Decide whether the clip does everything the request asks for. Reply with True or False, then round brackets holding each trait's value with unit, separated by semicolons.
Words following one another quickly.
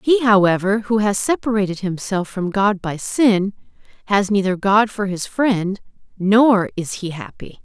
False (155 wpm)